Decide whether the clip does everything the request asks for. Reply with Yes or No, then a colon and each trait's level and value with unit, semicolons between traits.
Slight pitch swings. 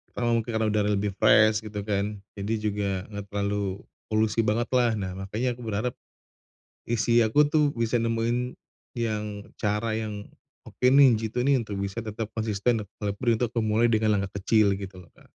Yes: narrow, 2.2 semitones